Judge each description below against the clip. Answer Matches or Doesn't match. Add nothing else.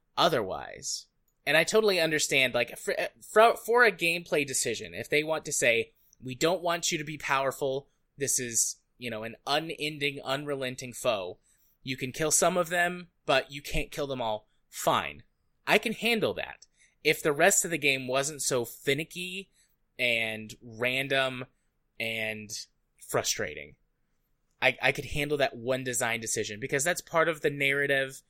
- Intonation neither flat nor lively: Matches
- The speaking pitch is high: Doesn't match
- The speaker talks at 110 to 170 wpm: Matches